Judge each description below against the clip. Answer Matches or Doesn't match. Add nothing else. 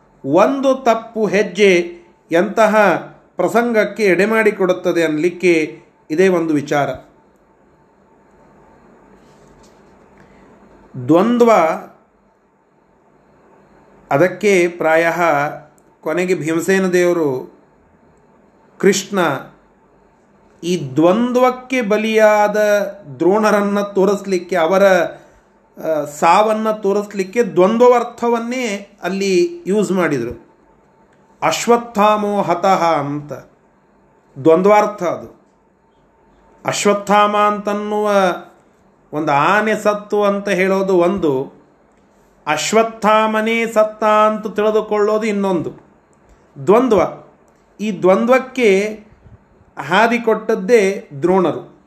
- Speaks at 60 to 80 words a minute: Matches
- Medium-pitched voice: Doesn't match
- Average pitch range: Matches